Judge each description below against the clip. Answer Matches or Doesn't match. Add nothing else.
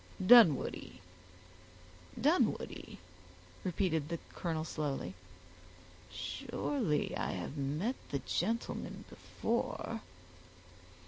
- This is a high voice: Doesn't match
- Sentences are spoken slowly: Matches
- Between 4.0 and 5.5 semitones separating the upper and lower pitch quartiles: Matches